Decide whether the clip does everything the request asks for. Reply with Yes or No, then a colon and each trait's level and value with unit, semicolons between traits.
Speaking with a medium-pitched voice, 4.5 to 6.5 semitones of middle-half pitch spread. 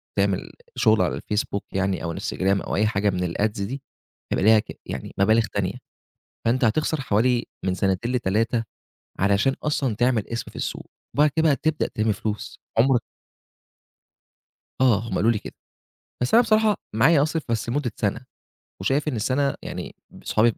No: low, 115 Hz; average, 4.9 semitones